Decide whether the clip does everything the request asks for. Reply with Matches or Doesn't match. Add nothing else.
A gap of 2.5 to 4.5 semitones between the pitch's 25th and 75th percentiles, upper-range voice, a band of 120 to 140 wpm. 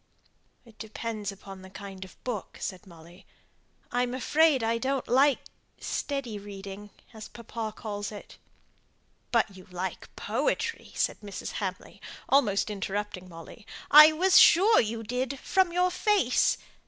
Doesn't match